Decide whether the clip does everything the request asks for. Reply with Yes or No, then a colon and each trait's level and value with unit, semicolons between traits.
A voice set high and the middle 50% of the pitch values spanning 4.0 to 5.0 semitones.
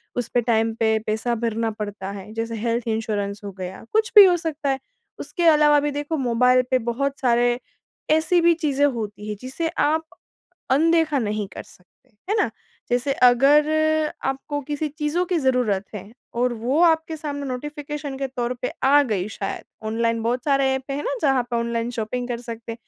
Yes: very high, 250 Hz; average, 4.4 semitones